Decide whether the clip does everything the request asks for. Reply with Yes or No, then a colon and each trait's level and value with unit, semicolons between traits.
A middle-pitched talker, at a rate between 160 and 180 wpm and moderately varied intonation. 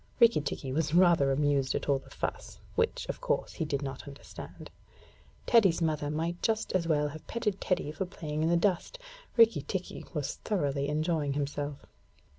Yes: medium, 155 Hz; average, 170 wpm; average, 4.2 semitones